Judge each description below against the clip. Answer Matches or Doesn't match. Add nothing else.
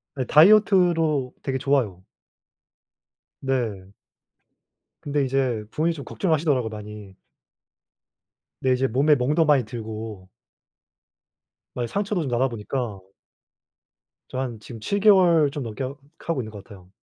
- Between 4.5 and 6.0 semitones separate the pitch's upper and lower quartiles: Matches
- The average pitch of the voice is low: Matches